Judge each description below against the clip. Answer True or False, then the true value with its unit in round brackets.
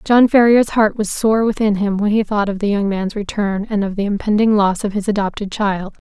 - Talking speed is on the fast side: True (240 wpm)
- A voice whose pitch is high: True (205 Hz)